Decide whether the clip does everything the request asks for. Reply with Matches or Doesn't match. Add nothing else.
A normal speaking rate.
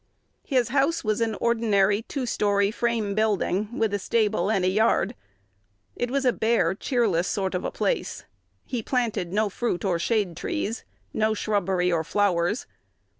Matches